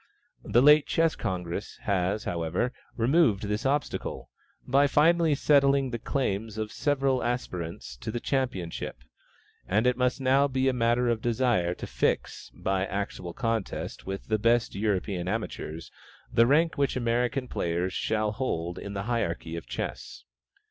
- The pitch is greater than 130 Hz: No, low, 115 Hz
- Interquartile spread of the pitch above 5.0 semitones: Yes, wide, 5.4 semitones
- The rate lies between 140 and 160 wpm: Yes, average, 155 wpm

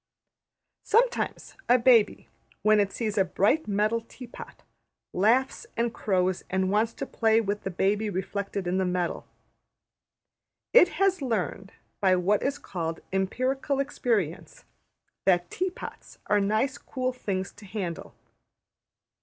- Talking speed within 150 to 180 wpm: No, slow, 135 wpm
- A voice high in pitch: Yes, high, 210 Hz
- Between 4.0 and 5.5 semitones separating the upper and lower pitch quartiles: Yes, average, 4.8 semitones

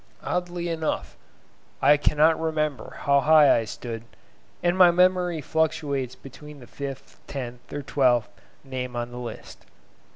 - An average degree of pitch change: Yes, average, 4.1 semitones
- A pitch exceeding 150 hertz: No, medium, 145 Hz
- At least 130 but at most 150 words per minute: Yes, slow, 135 wpm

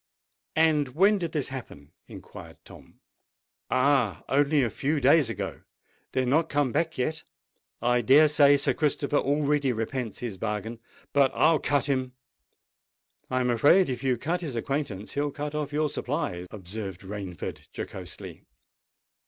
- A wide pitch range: No, average, 4.0 semitones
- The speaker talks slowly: No, average, 145 wpm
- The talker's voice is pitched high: No, low, 135 Hz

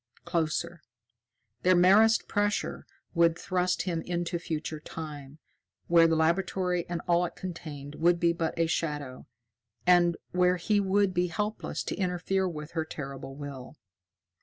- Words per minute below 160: Yes, average, 140 wpm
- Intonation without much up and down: Yes, narrow, 2.3 semitones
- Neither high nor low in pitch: Yes, medium, 170 Hz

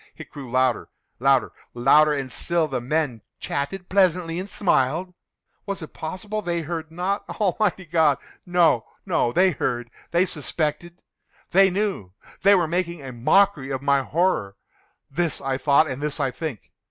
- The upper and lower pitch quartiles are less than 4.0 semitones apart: No, average, 5.0 semitones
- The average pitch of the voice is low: No, medium, 160 Hz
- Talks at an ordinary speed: No, slow, 130 wpm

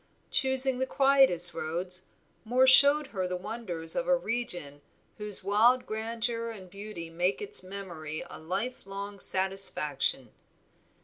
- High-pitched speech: Yes, high, 200 Hz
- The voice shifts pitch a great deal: Yes, wide, 5.7 semitones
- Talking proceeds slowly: Yes, slow, 130 wpm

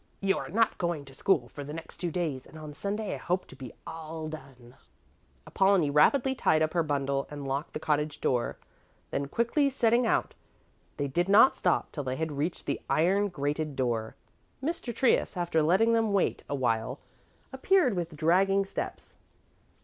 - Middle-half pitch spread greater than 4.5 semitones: Yes, wide, 5.6 semitones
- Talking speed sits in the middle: Yes, average, 180 wpm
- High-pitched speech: No, medium, 160 Hz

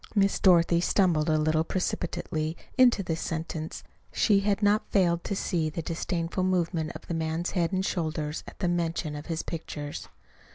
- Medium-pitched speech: Yes, medium, 170 Hz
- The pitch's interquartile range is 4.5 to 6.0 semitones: No, average, 2.8 semitones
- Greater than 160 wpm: Yes, average, 170 wpm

